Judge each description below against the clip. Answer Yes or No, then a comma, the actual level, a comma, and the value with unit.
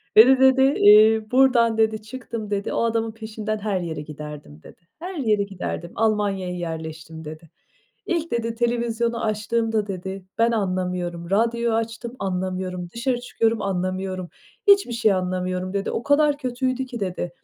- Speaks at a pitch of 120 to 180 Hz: No, high, 215 Hz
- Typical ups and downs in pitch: Yes, average, 4.1 semitones